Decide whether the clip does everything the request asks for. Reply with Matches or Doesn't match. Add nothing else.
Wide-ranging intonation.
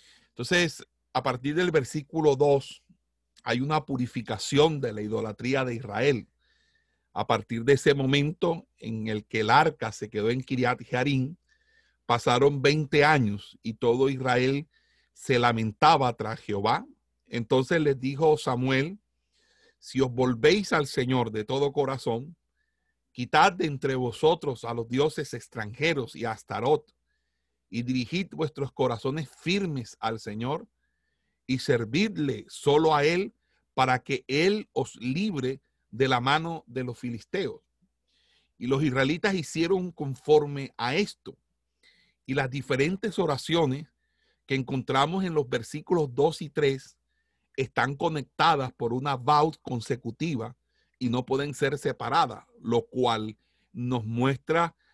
Doesn't match